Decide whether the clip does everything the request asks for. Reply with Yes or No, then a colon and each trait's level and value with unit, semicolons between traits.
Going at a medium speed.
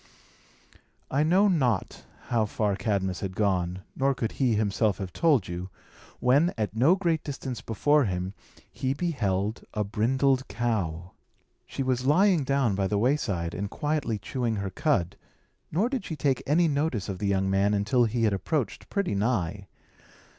Yes: average, 160 wpm